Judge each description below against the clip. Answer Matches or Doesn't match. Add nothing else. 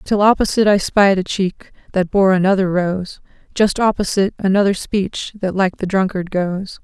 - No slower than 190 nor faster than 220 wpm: Doesn't match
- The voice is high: Matches